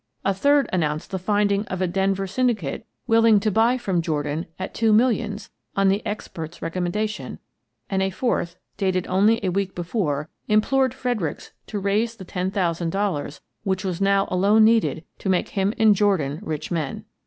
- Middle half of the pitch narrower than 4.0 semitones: Yes, average, 3.3 semitones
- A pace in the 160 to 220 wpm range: Yes, average, 175 wpm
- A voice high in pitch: Yes, high, 195 Hz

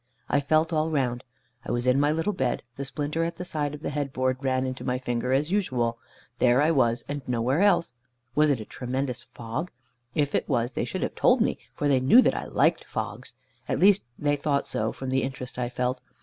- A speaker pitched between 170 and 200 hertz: No, low, 135 Hz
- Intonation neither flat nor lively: Yes, average, 3.2 semitones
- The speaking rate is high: Yes, fast, 225 wpm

